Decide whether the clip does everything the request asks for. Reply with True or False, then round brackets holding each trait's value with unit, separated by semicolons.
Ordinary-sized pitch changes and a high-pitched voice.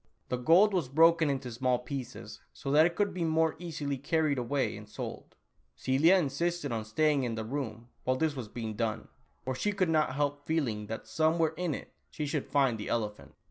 False (4.8 semitones; 140 Hz)